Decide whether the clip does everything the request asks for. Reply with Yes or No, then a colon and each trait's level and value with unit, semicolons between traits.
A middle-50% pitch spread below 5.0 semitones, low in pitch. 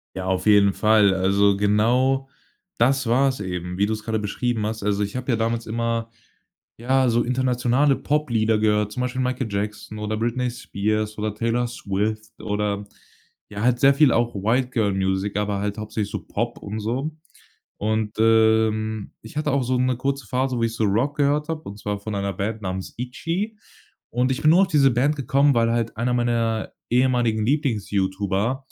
Yes: average, 3.5 semitones; low, 115 Hz